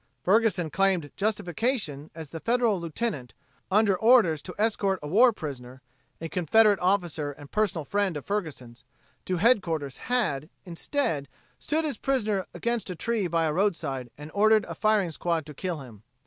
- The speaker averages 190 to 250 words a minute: No, average, 160 wpm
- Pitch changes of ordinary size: No, wide, 5.9 semitones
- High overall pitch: No, medium, 180 Hz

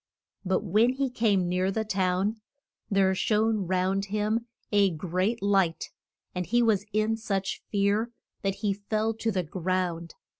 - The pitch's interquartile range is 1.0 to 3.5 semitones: Yes, average, 2.7 semitones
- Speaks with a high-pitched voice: Yes, high, 200 Hz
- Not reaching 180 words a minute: Yes, average, 150 wpm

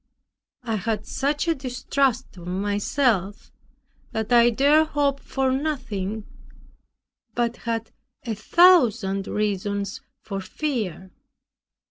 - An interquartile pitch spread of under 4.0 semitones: No, average, 5.1 semitones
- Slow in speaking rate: Yes, slow, 100 wpm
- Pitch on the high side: Yes, high, 230 Hz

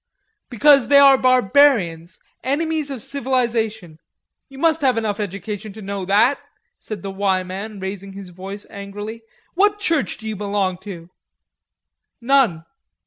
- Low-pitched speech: No, high, 215 Hz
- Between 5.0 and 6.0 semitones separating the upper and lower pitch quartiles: Yes, wide, 5.6 semitones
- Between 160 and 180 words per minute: No, average, 140 wpm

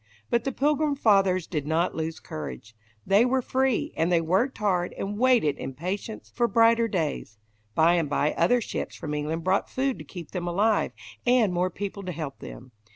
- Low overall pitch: No, medium, 185 Hz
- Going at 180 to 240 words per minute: Yes, average, 190 wpm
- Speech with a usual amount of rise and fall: No, wide, 6.3 semitones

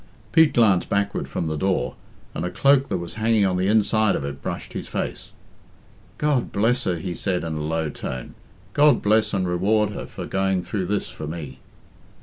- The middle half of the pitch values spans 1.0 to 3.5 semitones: No, average, 4.1 semitones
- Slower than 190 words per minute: No, average, 195 wpm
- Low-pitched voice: Yes, very low, 95 Hz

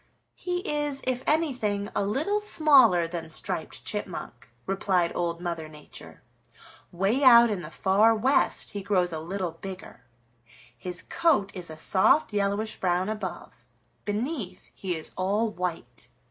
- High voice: Yes, high, 200 Hz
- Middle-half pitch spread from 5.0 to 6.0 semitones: Yes, wide, 5.5 semitones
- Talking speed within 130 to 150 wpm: Yes, average, 140 wpm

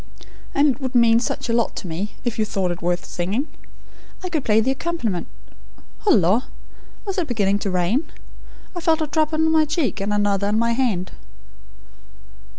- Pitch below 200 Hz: No, high, 230 Hz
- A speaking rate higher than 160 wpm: Yes, average, 180 wpm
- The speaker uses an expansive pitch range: Yes, wide, 7.3 semitones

